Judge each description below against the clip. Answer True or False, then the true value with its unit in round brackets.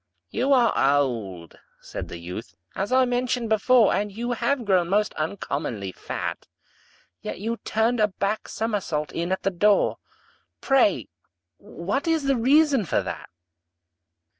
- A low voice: False (210 Hz)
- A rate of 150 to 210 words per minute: False (140 wpm)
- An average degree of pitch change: False (7.4 semitones)